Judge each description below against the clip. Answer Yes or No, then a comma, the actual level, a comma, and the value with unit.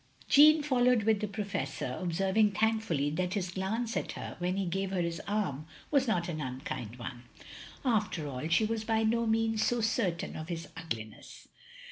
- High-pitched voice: Yes, high, 195 Hz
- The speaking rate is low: No, average, 175 wpm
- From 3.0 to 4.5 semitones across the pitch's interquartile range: No, average, 5.3 semitones